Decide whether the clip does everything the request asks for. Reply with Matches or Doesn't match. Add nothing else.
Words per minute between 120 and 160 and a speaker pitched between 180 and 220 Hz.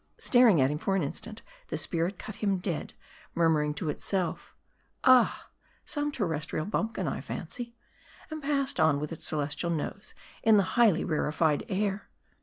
Matches